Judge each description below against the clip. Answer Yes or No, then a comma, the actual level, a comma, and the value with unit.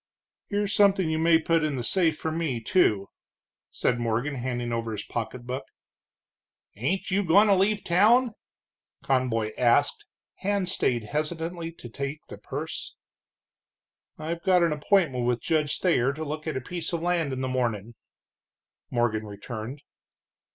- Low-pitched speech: No, medium, 150 Hz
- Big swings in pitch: Yes, wide, 6.1 semitones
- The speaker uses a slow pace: No, average, 150 wpm